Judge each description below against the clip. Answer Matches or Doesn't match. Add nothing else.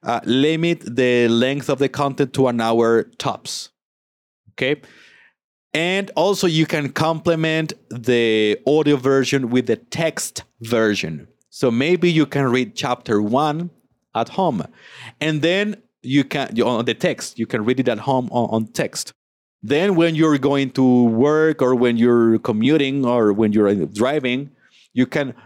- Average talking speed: Matches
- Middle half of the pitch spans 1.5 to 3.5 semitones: Doesn't match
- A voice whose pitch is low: Matches